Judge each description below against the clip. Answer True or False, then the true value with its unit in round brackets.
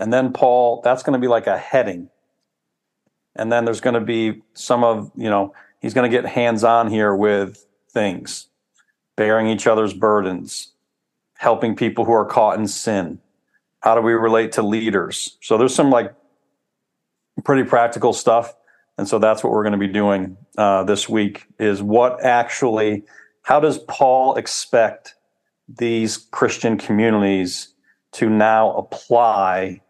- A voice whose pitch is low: True (110 Hz)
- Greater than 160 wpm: False (155 wpm)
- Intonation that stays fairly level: True (2.1 semitones)